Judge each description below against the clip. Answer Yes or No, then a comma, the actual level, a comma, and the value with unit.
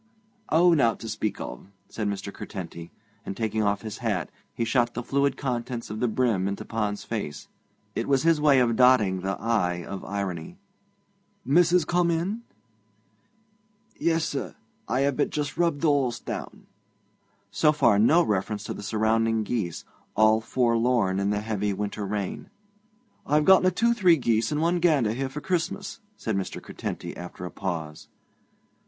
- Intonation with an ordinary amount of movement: No, wide, 6.4 semitones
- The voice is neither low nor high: No, low, 115 Hz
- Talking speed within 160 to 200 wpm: Yes, average, 165 wpm